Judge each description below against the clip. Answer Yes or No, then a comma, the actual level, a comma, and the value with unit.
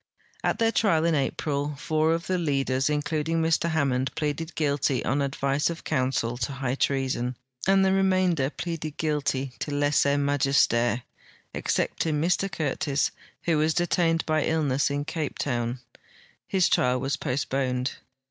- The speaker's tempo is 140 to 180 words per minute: Yes, average, 145 wpm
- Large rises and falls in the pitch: No, average, 3.2 semitones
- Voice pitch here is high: No, medium, 145 Hz